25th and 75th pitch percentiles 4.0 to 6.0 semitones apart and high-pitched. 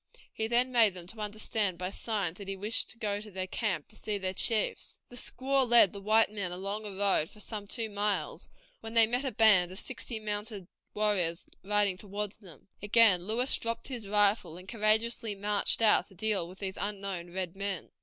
No: average, 2.7 semitones; high, 205 Hz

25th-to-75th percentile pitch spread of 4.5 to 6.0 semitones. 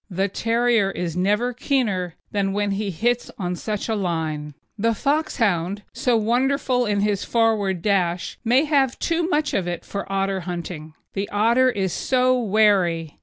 Yes: average, 4.9 semitones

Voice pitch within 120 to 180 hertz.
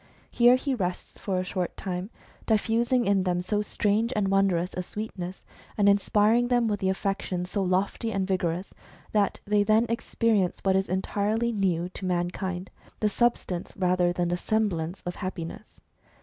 No: high, 195 Hz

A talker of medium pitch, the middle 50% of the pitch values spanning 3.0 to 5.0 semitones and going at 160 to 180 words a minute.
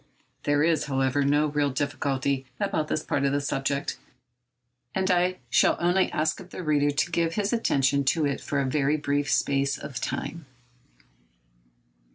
No: medium, 145 Hz; narrow, 2.6 semitones; average, 165 wpm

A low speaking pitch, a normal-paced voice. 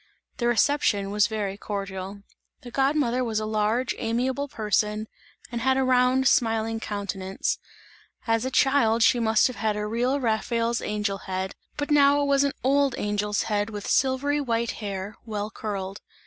No: high, 225 Hz; average, 165 wpm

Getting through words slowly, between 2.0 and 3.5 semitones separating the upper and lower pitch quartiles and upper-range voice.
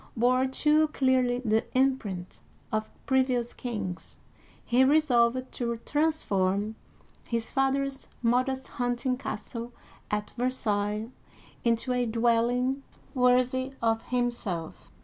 Yes: slow, 105 wpm; narrow, 2.5 semitones; high, 245 Hz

